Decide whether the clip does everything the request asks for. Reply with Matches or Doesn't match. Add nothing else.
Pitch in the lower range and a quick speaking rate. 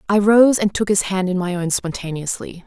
Doesn't match